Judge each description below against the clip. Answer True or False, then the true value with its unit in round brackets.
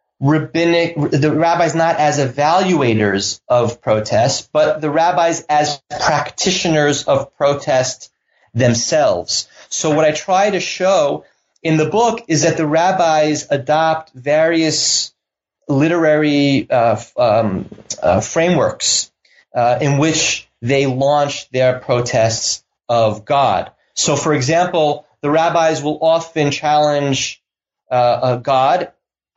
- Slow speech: True (115 wpm)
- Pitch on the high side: False (150 Hz)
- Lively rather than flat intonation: False (2.7 semitones)